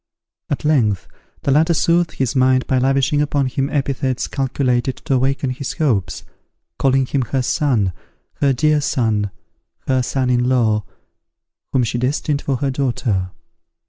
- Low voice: Yes, low, 130 Hz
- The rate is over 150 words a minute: No, average, 145 wpm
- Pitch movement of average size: No, narrow, 2.3 semitones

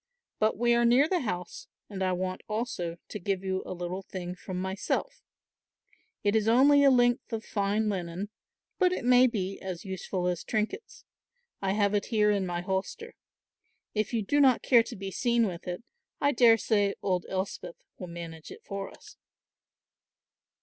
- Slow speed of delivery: No, average, 175 wpm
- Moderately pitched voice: No, high, 200 Hz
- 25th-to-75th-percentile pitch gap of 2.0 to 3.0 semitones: No, average, 4.2 semitones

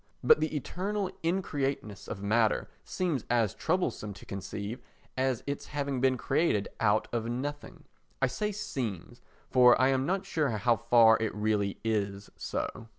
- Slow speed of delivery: No, average, 150 wpm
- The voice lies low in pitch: Yes, low, 125 Hz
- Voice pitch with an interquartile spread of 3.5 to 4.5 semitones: No, average, 5.2 semitones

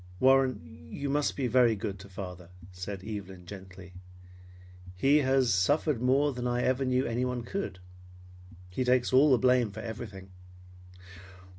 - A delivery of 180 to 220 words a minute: No, average, 145 wpm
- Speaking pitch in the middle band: No, low, 120 Hz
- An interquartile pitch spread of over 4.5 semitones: Yes, average, 5.1 semitones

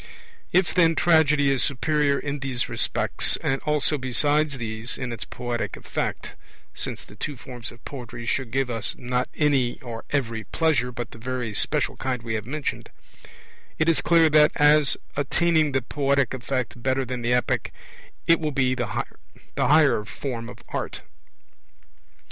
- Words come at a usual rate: Yes, average, 160 wpm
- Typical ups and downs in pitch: Yes, average, 3.5 semitones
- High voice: No, low, 135 Hz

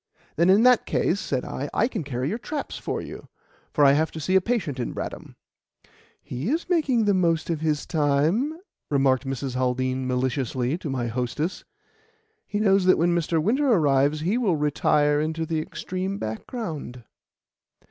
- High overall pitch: No, medium, 155 Hz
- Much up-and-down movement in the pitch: Yes, wide, 6.4 semitones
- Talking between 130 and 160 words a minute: No, average, 170 wpm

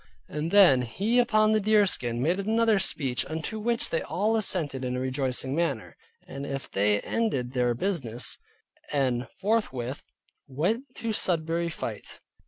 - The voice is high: No, medium, 165 Hz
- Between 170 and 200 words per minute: No, average, 145 wpm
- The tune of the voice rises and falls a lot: Yes, wide, 8.7 semitones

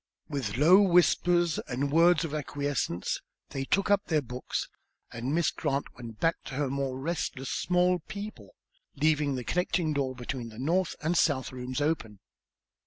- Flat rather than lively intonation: No, average, 4.8 semitones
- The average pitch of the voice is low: No, medium, 145 Hz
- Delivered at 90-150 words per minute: No, average, 160 wpm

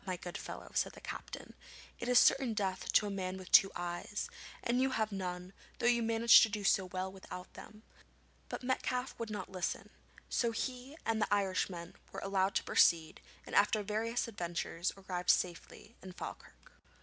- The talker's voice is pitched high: Yes, high, 200 Hz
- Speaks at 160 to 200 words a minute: Yes, average, 180 wpm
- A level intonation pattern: No, average, 3.8 semitones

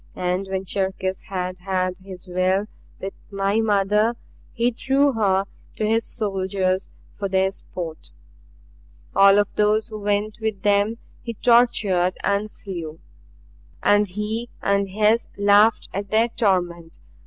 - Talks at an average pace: No, slow, 130 wpm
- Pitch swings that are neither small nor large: No, narrow, 2.2 semitones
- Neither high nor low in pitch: No, high, 200 Hz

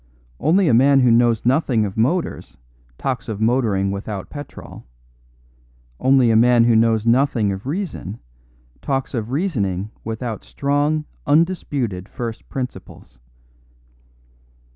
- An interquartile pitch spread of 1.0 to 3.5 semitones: No, average, 4.1 semitones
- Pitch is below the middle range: Yes, low, 120 Hz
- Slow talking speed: Yes, slow, 120 wpm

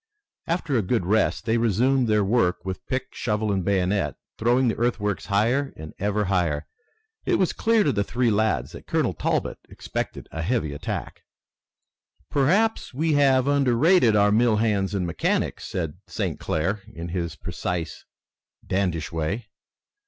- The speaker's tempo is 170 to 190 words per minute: No, average, 150 wpm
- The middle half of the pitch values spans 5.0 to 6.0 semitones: Yes, wide, 5.4 semitones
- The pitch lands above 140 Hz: No, low, 105 Hz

